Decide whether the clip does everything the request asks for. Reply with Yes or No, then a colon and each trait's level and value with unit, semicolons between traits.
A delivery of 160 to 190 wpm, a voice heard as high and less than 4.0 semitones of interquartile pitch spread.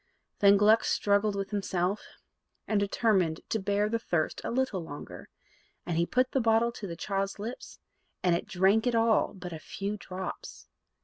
Yes: average, 175 wpm; high, 200 Hz; average, 3.1 semitones